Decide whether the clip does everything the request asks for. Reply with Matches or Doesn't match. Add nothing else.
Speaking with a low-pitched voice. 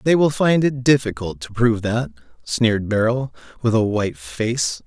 Matches